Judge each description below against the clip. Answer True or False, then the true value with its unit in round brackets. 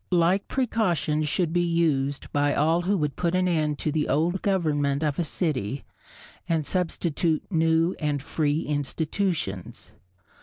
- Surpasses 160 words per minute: False (145 wpm)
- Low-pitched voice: False (160 Hz)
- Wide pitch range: False (3.1 semitones)